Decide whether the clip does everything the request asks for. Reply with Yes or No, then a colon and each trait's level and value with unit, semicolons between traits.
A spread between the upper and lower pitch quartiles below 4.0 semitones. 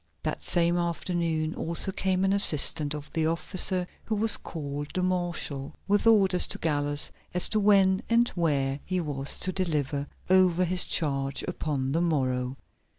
No: average, 4.3 semitones